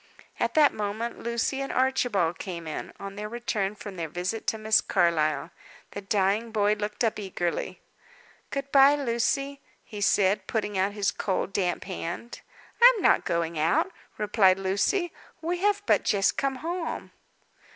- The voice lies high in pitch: Yes, high, 210 Hz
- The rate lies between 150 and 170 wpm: Yes, average, 160 wpm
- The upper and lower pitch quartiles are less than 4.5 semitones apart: No, average, 5.3 semitones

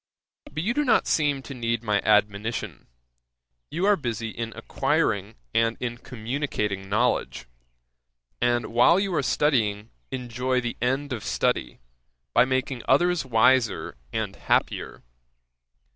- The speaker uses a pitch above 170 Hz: No, low, 120 Hz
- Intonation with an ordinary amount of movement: Yes, average, 3.6 semitones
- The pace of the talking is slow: Yes, slow, 130 wpm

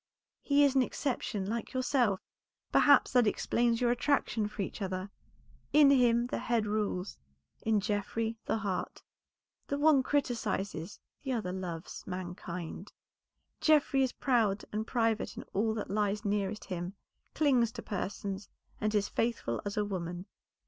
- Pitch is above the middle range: Yes, high, 215 Hz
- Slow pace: No, average, 145 wpm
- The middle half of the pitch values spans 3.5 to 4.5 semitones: Yes, average, 3.8 semitones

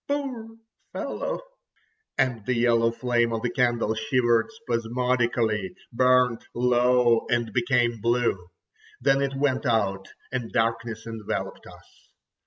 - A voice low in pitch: Yes, low, 120 Hz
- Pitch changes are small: Yes, narrow, 1.8 semitones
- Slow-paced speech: Yes, slow, 110 wpm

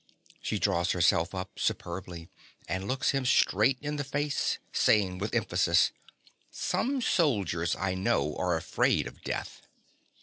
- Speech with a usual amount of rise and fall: No, wide, 7.0 semitones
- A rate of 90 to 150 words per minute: Yes, slow, 135 wpm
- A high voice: No, low, 100 Hz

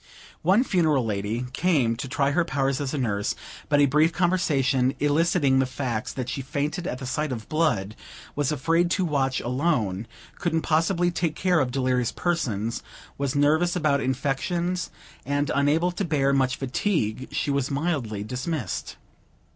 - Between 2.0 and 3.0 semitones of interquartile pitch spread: No, average, 4.4 semitones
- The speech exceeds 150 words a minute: Yes, average, 160 wpm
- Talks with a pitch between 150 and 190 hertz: No, medium, 140 Hz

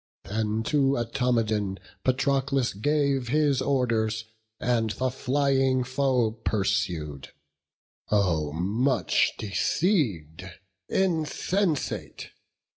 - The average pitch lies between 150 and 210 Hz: No, low, 125 Hz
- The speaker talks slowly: Yes, slow, 75 wpm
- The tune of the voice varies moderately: Yes, average, 4.9 semitones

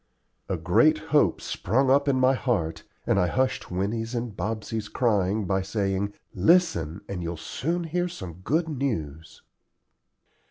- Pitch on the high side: No, low, 110 Hz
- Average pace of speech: Yes, average, 145 wpm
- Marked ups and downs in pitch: Yes, wide, 6.8 semitones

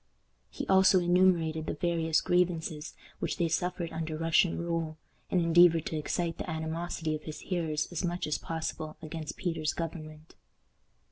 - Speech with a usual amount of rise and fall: No, narrow, 1.7 semitones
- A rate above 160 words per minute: No, average, 150 wpm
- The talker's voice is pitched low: No, medium, 165 Hz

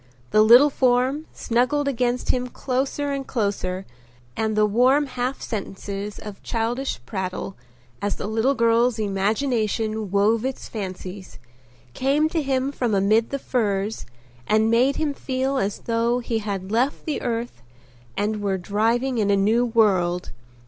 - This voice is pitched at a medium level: No, high, 230 Hz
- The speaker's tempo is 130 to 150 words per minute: Yes, average, 145 wpm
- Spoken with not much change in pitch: No, average, 4.0 semitones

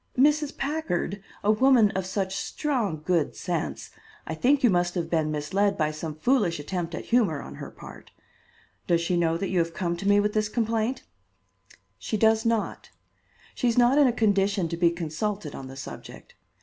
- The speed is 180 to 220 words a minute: Yes, average, 190 wpm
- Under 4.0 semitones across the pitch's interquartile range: No, average, 5.2 semitones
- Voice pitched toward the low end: No, high, 195 Hz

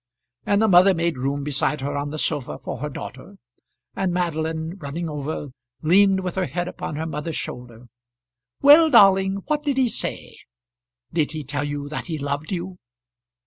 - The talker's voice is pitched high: No, medium, 160 Hz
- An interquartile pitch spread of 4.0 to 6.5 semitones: Yes, average, 4.8 semitones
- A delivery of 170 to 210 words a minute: Yes, average, 175 wpm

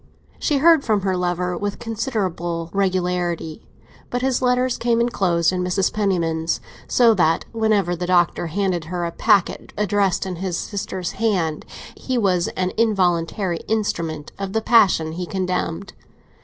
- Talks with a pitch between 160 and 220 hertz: Yes, medium, 185 Hz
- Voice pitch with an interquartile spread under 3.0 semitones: No, average, 3.7 semitones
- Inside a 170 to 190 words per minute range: No, average, 145 wpm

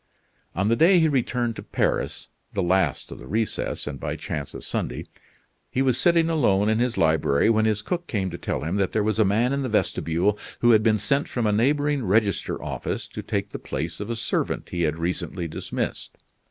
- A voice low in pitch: Yes, low, 110 Hz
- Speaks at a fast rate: Yes, fast, 215 wpm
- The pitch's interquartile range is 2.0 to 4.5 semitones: No, average, 4.9 semitones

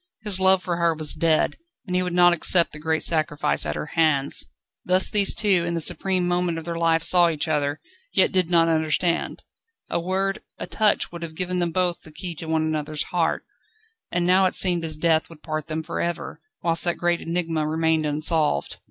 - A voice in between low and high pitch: Yes, medium, 170 Hz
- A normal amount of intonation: No, narrow, 2.1 semitones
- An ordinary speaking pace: No, fast, 215 wpm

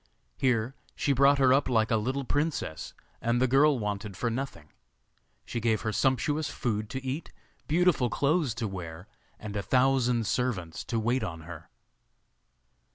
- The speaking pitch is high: No, low, 120 Hz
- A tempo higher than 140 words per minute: Yes, average, 160 wpm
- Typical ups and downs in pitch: Yes, average, 4.2 semitones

